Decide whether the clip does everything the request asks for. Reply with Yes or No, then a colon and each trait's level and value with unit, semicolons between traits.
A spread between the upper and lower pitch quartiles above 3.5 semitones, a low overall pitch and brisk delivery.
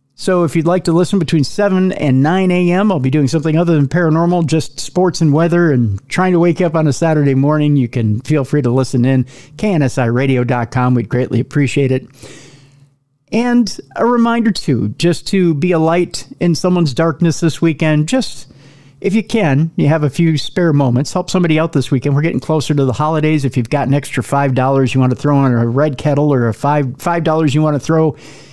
No: average, 3.9 semitones; medium, 150 Hz; fast, 210 wpm